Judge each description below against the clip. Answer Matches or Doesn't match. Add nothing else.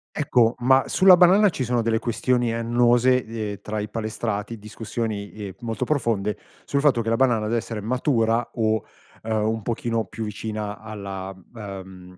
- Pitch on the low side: Matches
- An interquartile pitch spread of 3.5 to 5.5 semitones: Doesn't match